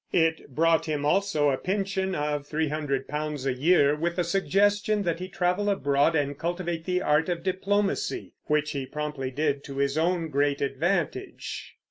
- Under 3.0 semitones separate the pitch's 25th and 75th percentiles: No, average, 4.0 semitones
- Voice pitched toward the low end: No, medium, 160 Hz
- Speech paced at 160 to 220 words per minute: Yes, average, 170 wpm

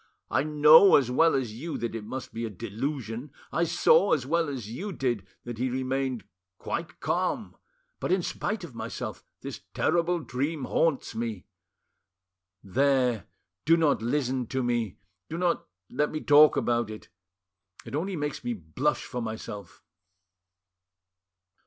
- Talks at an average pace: Yes, average, 150 wpm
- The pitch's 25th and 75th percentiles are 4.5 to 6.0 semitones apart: Yes, average, 5.0 semitones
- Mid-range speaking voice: No, low, 130 Hz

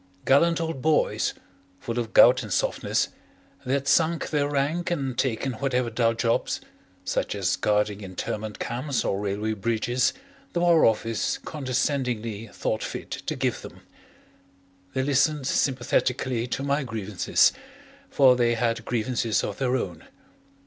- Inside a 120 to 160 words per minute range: Yes, average, 140 wpm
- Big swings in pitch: No, average, 3.8 semitones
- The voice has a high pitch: No, low, 125 Hz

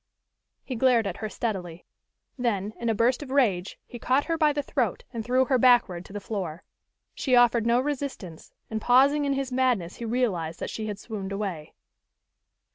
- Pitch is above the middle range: Yes, high, 235 Hz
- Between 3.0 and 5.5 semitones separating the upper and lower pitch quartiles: Yes, average, 4.7 semitones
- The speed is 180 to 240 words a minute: Yes, average, 190 wpm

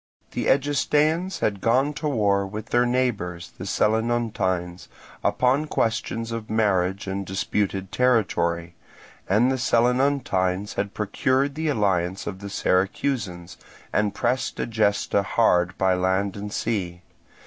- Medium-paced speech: No, slow, 125 wpm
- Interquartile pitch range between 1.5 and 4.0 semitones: No, average, 4.7 semitones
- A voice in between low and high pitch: No, low, 105 Hz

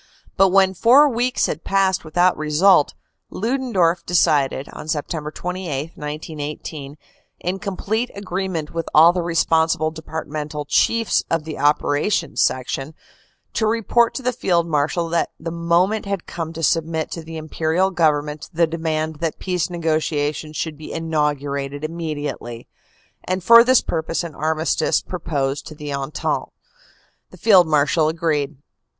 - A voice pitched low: No, medium, 160 Hz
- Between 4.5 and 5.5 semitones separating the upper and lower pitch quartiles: No, average, 3.3 semitones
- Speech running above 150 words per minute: No, average, 140 wpm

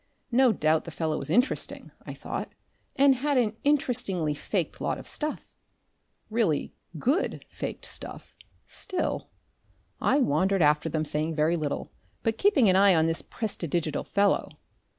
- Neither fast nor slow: Yes, average, 145 wpm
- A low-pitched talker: No, high, 190 Hz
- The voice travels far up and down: Yes, wide, 8.1 semitones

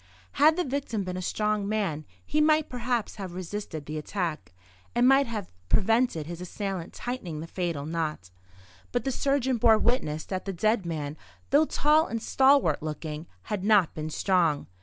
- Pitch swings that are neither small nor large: No, wide, 7.0 semitones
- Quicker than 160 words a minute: Yes, average, 170 wpm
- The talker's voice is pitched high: Yes, high, 200 Hz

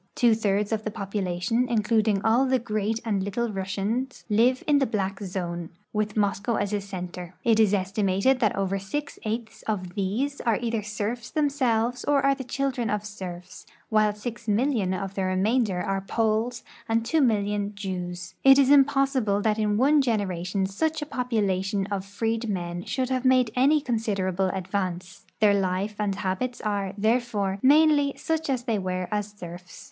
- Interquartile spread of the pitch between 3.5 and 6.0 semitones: Yes, average, 3.9 semitones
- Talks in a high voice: Yes, high, 210 Hz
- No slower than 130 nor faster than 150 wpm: No, average, 170 wpm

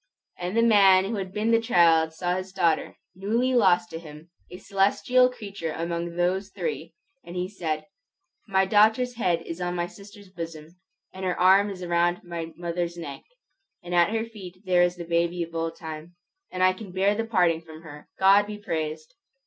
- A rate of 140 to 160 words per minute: No, average, 190 wpm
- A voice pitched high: No, medium, 180 Hz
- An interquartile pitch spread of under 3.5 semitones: Yes, average, 3.0 semitones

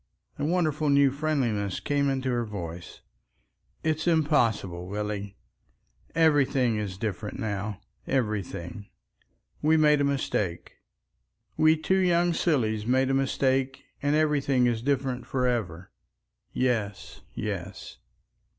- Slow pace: Yes, slow, 110 wpm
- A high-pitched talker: No, low, 130 Hz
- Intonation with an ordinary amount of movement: No, wide, 5.9 semitones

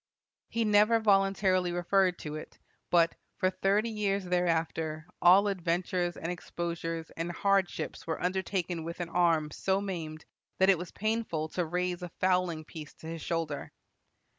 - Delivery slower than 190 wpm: Yes, average, 150 wpm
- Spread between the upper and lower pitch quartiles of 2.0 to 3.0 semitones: Yes, average, 2.7 semitones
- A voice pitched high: No, medium, 180 Hz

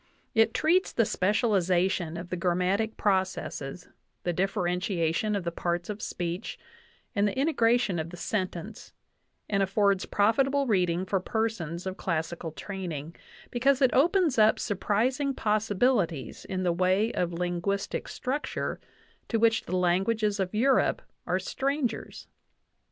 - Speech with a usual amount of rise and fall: Yes, average, 4.3 semitones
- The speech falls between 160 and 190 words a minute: No, slow, 135 wpm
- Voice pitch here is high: Yes, high, 195 Hz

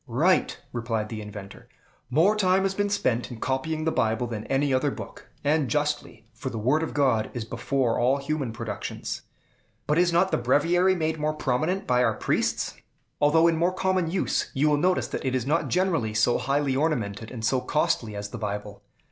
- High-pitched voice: No, medium, 140 Hz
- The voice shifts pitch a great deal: Yes, wide, 5.9 semitones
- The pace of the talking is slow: No, average, 195 wpm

